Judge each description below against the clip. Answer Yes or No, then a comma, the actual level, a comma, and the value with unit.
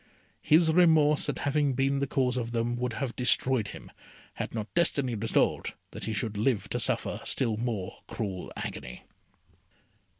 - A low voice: Yes, low, 125 Hz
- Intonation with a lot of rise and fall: No, average, 3.8 semitones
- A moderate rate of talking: Yes, average, 160 wpm